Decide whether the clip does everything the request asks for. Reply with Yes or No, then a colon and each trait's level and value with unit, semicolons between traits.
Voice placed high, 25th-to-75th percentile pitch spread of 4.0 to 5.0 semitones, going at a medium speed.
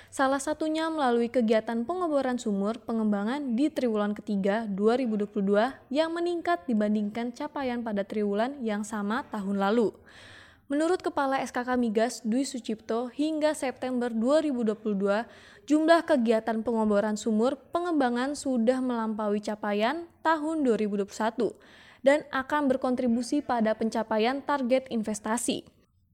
Yes: high, 240 Hz; average, 4.3 semitones; average, 110 wpm